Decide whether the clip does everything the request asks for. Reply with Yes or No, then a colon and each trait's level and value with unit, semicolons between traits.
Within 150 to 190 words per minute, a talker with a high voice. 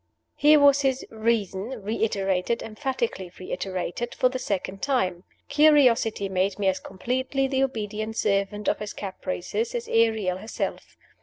No: slow, 135 wpm; high, 220 Hz